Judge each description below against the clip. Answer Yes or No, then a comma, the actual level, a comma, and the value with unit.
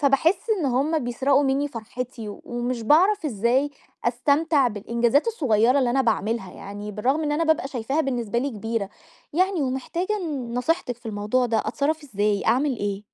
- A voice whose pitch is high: Yes, very high, 255 Hz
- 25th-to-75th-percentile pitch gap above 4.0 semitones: Yes, average, 4.4 semitones